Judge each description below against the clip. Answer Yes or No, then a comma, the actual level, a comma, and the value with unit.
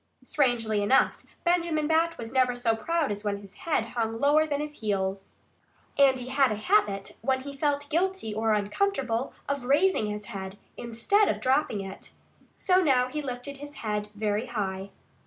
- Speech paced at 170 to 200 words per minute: Yes, average, 175 wpm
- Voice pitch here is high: Yes, very high, 250 Hz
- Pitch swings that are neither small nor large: No, wide, 5.7 semitones